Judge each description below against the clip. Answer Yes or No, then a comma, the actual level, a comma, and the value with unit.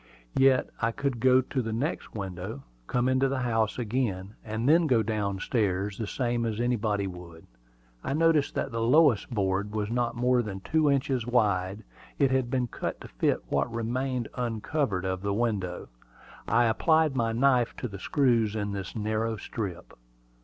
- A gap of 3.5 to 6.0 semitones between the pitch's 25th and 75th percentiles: Yes, average, 3.9 semitones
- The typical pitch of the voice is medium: No, low, 115 Hz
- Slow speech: No, average, 175 wpm